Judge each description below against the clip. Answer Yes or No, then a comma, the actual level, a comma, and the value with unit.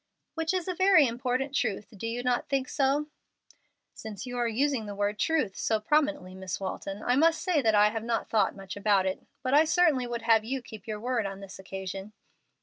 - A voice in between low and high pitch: No, high, 235 Hz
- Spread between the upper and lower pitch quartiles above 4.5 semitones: Yes, average, 5.3 semitones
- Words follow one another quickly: Yes, fast, 215 wpm